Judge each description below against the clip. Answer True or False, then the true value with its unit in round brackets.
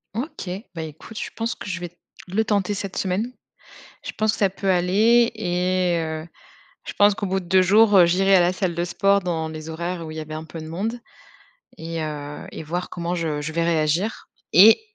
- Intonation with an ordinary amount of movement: True (3.5 semitones)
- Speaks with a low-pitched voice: False (180 Hz)